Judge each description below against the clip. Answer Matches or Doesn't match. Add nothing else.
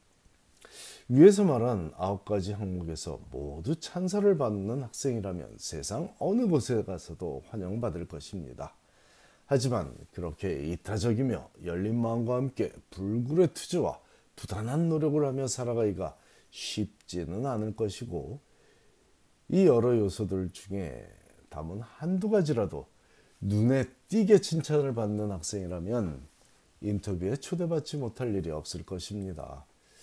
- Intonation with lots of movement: Matches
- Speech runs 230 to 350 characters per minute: Matches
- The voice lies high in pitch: Doesn't match